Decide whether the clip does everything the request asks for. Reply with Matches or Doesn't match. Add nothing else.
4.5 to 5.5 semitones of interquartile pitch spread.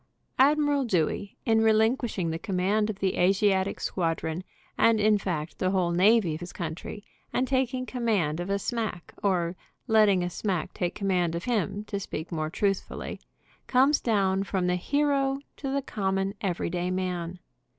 Doesn't match